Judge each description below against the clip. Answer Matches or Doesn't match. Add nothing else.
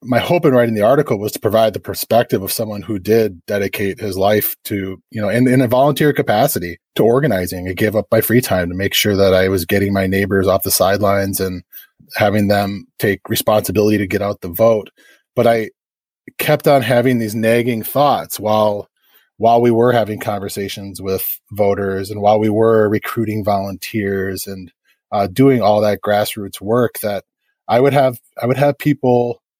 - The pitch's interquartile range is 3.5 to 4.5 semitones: Doesn't match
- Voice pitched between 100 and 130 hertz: Matches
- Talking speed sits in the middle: Matches